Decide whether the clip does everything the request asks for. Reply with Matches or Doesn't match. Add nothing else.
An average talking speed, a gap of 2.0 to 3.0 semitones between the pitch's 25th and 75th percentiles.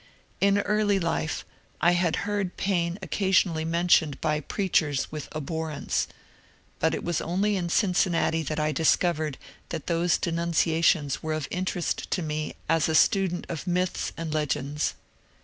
Matches